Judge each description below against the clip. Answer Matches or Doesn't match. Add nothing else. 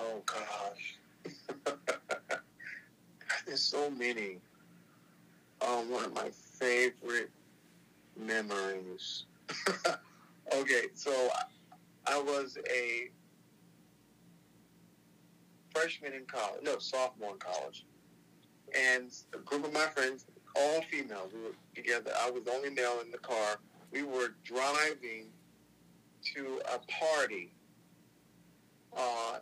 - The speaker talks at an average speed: Doesn't match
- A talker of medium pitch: Doesn't match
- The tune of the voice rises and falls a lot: Doesn't match